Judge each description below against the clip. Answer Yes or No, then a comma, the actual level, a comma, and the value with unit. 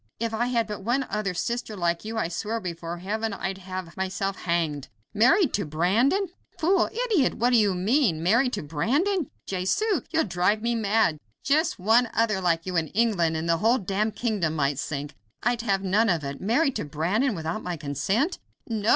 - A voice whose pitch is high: Yes, high, 205 Hz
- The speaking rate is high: No, average, 190 wpm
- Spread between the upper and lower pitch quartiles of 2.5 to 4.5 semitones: No, wide, 5.6 semitones